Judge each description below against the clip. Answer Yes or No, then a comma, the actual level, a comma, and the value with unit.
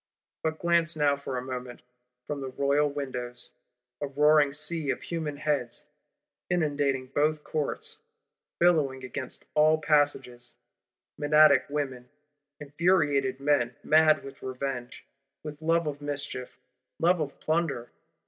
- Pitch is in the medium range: Yes, medium, 145 Hz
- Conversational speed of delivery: No, slow, 120 wpm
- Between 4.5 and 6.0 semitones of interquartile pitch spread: No, average, 2.8 semitones